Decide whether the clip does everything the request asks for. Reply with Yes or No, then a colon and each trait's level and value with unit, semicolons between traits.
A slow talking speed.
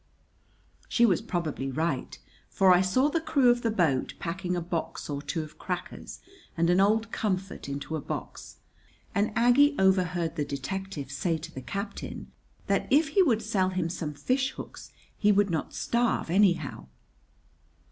No: average, 160 wpm